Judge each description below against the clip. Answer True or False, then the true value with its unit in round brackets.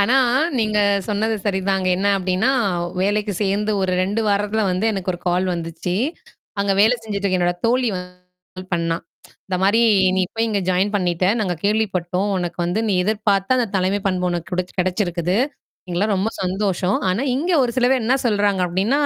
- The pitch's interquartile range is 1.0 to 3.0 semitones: True (2.6 semitones)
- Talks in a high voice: True (195 Hz)